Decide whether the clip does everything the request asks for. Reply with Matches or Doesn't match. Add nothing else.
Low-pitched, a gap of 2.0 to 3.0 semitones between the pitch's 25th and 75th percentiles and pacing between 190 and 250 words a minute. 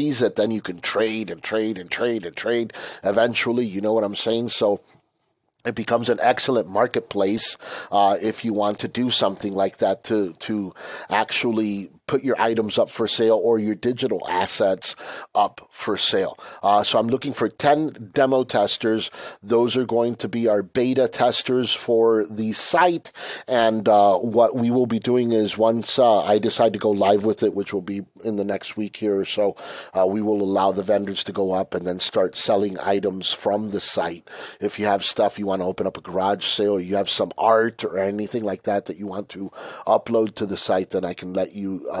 Matches